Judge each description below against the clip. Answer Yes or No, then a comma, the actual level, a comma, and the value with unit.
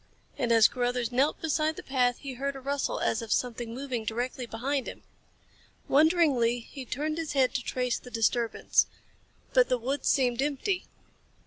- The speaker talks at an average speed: Yes, average, 165 wpm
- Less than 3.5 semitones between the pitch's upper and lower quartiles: Yes, average, 2.8 semitones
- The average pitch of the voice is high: Yes, very high, 255 Hz